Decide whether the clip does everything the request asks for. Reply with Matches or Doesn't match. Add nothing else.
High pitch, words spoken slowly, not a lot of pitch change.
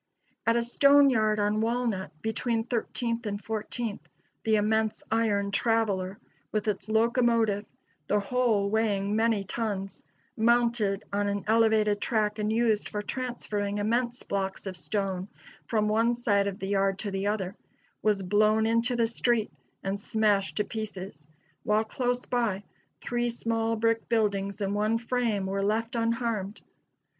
Doesn't match